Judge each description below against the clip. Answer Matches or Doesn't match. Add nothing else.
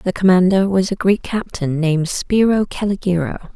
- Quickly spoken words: Doesn't match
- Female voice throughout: Matches